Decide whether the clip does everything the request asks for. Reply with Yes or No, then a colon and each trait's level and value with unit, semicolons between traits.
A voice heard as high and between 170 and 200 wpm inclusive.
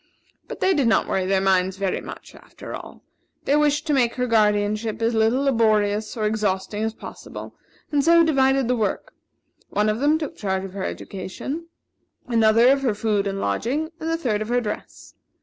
Yes: high, 225 Hz; average, 190 wpm